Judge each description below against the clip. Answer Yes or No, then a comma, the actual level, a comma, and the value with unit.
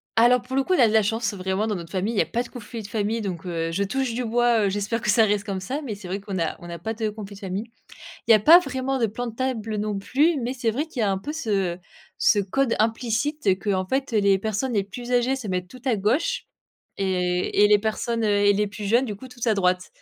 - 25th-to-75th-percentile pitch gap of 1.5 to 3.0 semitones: No, average, 3.6 semitones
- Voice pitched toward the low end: No, high, 220 Hz